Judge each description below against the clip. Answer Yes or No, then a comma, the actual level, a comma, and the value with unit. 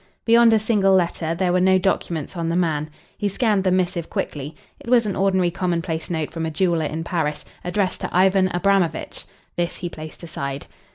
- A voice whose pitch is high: No, medium, 175 Hz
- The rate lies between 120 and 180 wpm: No, average, 190 wpm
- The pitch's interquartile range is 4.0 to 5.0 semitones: No, average, 2.8 semitones